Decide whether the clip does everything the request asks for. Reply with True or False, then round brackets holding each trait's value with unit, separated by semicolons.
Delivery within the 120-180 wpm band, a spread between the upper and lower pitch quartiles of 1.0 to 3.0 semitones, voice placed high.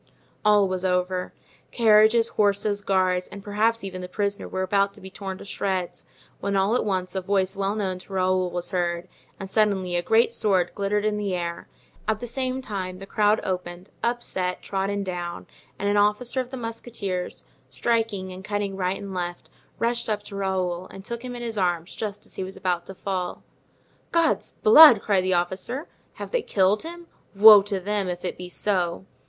False (195 wpm; 2.5 semitones; 195 Hz)